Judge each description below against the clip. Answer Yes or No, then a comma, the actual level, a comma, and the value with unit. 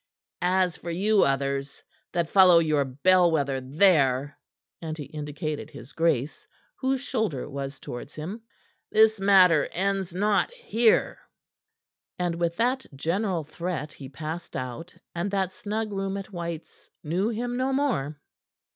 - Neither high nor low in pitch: Yes, medium, 170 Hz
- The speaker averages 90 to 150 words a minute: Yes, average, 140 wpm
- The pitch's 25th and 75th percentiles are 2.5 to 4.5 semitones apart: No, average, 5.2 semitones